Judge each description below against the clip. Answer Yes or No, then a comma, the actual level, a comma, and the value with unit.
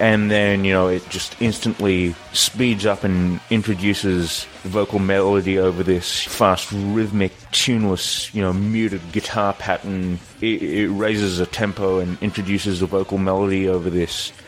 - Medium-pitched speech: No, low, 100 Hz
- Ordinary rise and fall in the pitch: No, narrow, 2.2 semitones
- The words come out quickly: No, average, 145 wpm